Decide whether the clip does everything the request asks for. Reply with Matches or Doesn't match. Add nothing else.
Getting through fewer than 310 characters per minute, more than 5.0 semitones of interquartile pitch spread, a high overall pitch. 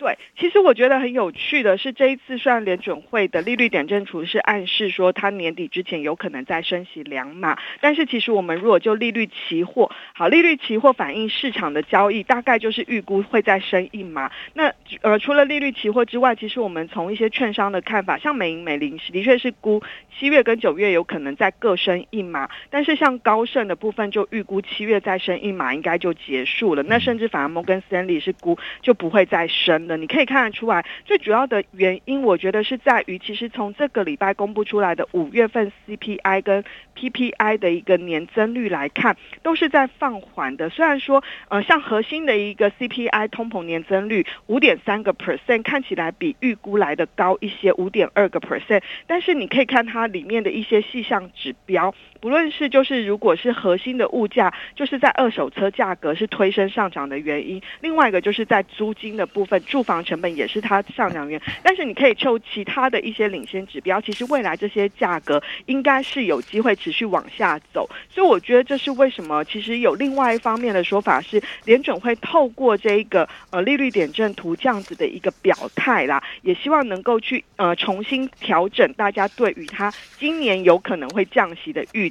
Doesn't match